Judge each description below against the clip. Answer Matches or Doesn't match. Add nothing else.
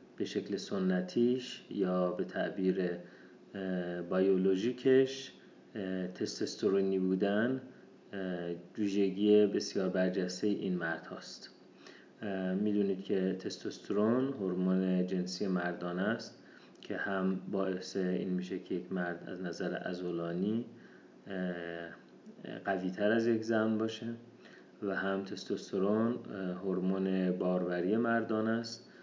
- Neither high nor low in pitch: Doesn't match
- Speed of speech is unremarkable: Doesn't match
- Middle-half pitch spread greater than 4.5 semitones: Doesn't match